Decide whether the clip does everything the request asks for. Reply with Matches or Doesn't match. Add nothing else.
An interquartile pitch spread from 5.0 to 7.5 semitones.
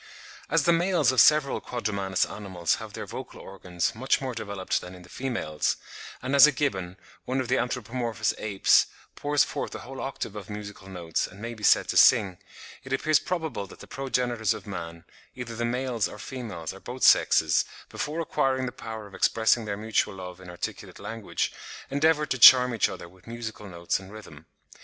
Matches